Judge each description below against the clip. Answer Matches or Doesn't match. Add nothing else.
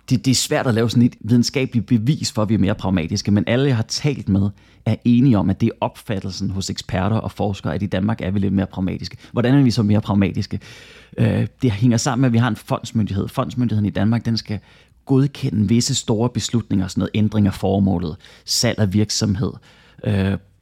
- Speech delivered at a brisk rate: Doesn't match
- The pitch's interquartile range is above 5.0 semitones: Doesn't match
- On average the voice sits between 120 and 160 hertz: Doesn't match